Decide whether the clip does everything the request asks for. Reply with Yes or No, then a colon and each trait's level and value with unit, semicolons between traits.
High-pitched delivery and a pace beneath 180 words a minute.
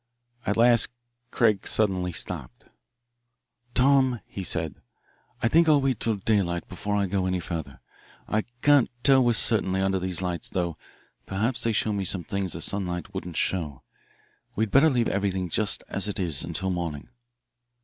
No: very low, 95 Hz; average, 160 wpm